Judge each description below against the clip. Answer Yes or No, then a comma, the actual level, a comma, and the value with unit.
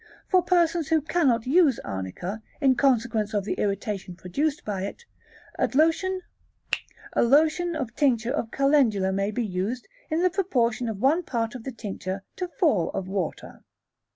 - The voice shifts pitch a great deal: Yes, wide, 7.4 semitones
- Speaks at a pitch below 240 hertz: No, high, 245 Hz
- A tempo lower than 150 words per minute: No, average, 155 wpm